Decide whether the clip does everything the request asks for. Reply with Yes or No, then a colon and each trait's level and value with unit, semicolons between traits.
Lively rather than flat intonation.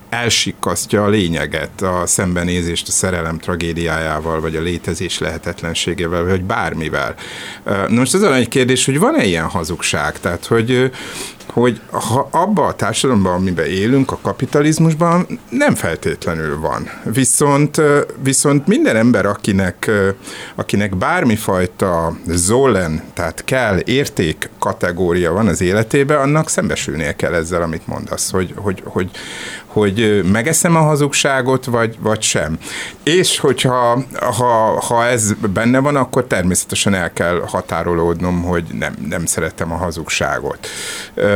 Yes: wide, 7.1 semitones